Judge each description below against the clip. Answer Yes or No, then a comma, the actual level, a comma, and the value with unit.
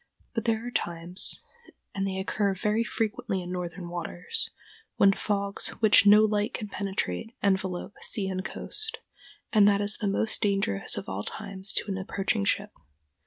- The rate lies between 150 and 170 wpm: Yes, average, 160 wpm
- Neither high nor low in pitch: No, high, 200 Hz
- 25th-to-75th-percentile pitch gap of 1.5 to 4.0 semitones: Yes, narrow, 2.4 semitones